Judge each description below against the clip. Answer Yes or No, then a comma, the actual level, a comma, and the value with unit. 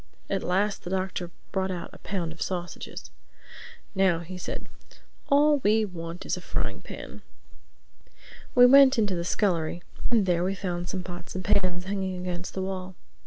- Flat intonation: Yes, narrow, 1.9 semitones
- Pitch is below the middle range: No, medium, 185 Hz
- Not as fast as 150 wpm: No, average, 165 wpm